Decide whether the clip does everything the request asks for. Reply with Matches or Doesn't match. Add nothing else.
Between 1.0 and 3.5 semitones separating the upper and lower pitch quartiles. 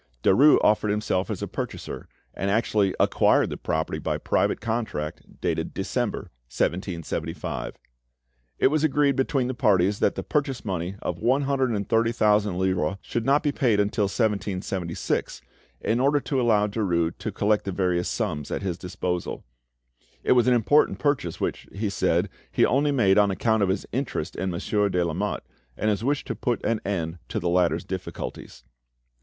Doesn't match